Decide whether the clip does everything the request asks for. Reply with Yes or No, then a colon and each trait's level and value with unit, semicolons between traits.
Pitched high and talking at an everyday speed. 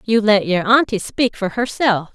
Yes: high, 215 Hz; average, 195 wpm